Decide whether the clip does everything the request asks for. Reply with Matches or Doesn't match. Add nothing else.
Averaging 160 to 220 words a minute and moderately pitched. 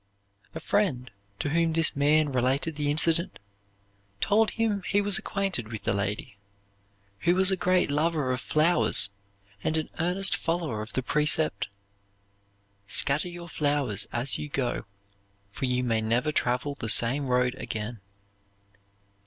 Doesn't match